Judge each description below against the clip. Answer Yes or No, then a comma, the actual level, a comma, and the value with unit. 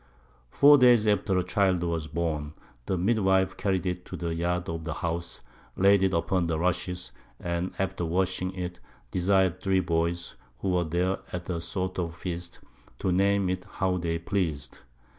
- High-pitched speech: No, very low, 90 Hz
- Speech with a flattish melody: Yes, narrow, 2.0 semitones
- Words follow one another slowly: No, average, 165 wpm